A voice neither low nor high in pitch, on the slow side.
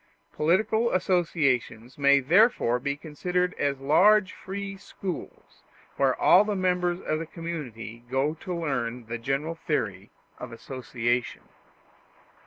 Yes: medium, 150 Hz; slow, 120 wpm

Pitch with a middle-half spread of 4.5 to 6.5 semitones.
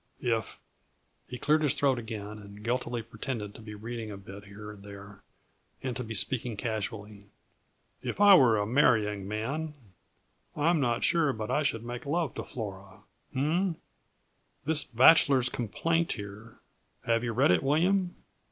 Yes: average, 5.1 semitones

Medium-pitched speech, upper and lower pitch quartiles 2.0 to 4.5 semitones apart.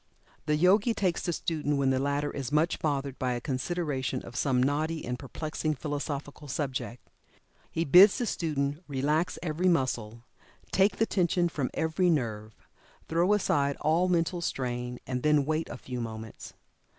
Yes: medium, 145 Hz; average, 4.2 semitones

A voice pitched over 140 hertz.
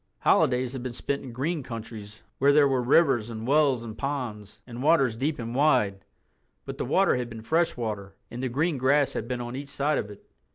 No: low, 125 Hz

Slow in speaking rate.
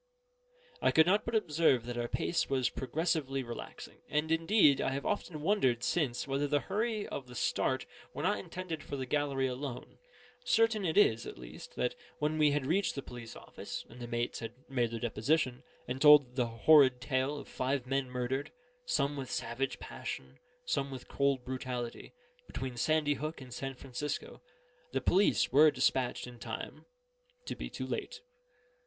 No: average, 175 wpm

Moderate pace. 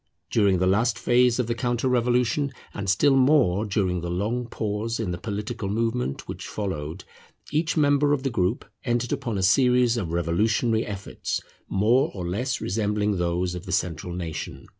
Yes: average, 170 wpm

